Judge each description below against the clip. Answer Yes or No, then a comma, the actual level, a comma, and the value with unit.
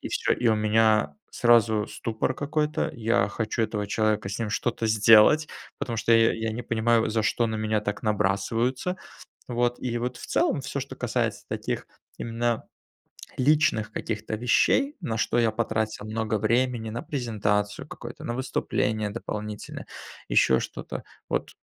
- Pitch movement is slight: Yes, narrow, 1.8 semitones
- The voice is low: Yes, low, 110 Hz